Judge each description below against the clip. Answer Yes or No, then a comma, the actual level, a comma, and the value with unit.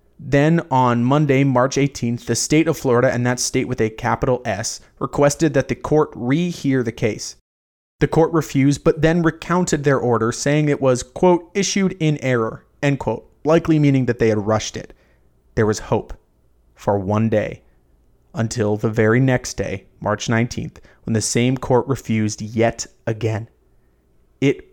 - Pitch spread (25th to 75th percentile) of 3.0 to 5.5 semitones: Yes, average, 4.8 semitones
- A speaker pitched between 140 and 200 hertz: No, low, 125 Hz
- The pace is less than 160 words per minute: No, average, 165 wpm